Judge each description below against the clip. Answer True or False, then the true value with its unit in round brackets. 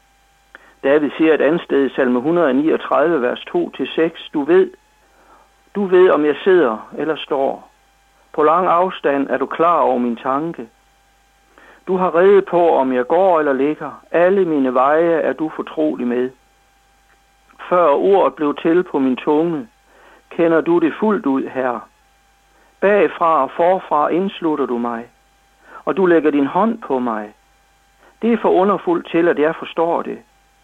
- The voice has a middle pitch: True (165 Hz)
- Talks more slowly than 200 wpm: True (155 wpm)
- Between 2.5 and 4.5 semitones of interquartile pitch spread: False (4.9 semitones)